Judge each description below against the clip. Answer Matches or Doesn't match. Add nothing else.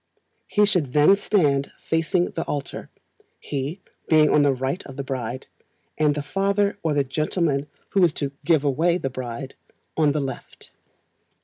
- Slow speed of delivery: Doesn't match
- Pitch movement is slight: Doesn't match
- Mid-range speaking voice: Matches